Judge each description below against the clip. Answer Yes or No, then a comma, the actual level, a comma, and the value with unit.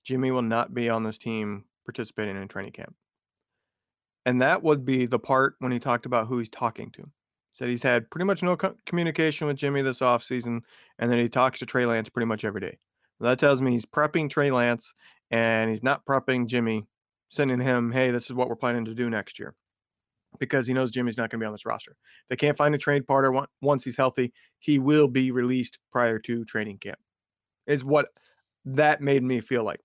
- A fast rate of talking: Yes, fast, 220 wpm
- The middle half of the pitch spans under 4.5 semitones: Yes, average, 2.7 semitones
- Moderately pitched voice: No, low, 125 Hz